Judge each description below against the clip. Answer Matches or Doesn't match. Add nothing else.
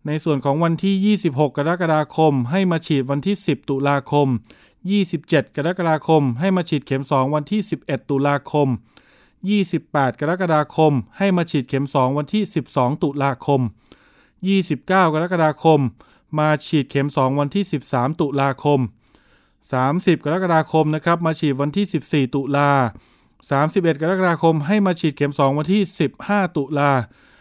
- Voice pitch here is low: Doesn't match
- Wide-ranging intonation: Doesn't match